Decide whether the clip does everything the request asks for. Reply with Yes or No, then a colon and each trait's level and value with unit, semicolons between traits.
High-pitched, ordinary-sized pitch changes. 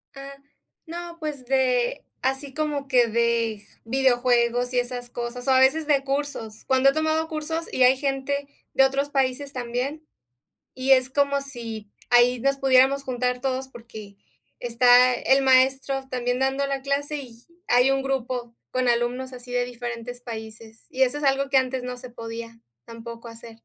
No: very high, 255 Hz; narrow, 2.1 semitones